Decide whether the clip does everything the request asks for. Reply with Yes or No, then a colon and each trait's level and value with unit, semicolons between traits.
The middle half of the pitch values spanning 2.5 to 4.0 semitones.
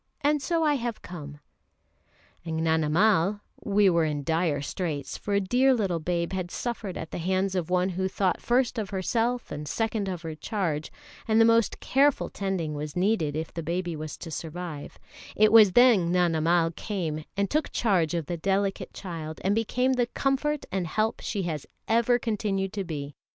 No: average, 5.2 semitones